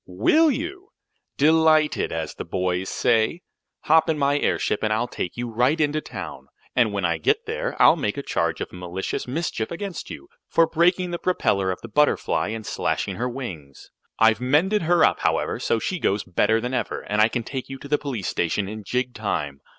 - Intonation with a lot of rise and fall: Yes, wide, 7.6 semitones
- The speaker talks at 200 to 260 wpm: Yes, fast, 205 wpm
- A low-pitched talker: Yes, low, 125 Hz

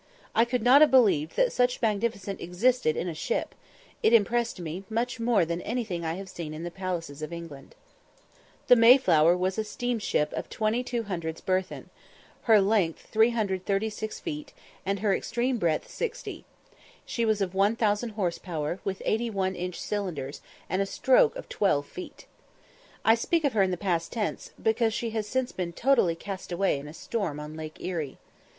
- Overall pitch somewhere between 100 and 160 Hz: No, high, 200 Hz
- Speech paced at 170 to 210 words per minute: Yes, average, 175 wpm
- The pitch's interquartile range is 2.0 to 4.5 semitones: No, average, 5.1 semitones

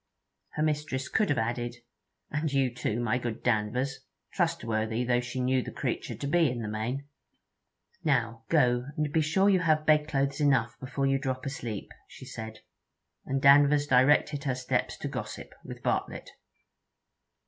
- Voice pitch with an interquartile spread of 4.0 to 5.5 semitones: No, average, 3.4 semitones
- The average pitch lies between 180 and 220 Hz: No, low, 130 Hz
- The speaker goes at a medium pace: Yes, average, 160 wpm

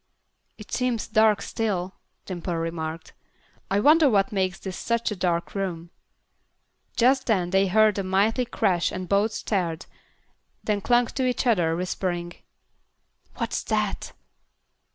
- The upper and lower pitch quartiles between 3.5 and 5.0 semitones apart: Yes, average, 4.0 semitones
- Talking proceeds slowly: Yes, slow, 130 wpm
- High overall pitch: Yes, high, 195 Hz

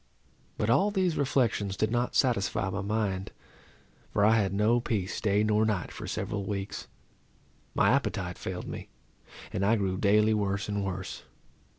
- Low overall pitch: Yes, low, 105 Hz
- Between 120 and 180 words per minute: Yes, average, 160 wpm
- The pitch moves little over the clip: Yes, narrow, 2.3 semitones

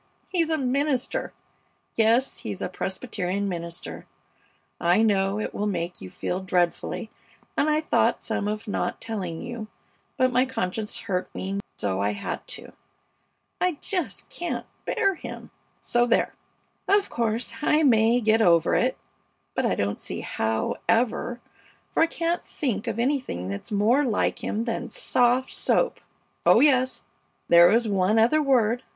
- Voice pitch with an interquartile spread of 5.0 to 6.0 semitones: Yes, wide, 5.4 semitones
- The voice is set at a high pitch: Yes, high, 225 Hz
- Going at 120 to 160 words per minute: Yes, average, 150 wpm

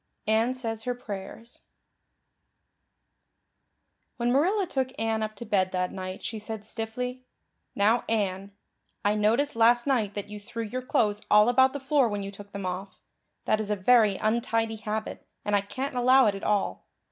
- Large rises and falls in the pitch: No, average, 3.2 semitones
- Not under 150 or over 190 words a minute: Yes, average, 170 wpm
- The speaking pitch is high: Yes, high, 220 Hz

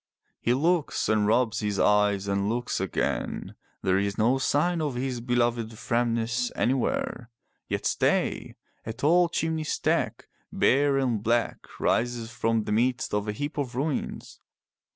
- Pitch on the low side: Yes, low, 120 Hz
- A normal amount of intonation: Yes, average, 3.6 semitones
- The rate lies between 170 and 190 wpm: No, average, 145 wpm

